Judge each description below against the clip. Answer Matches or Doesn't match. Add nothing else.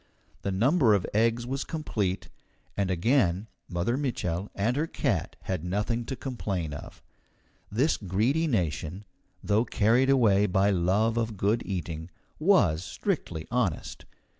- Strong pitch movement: Doesn't match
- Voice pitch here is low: Matches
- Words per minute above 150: Doesn't match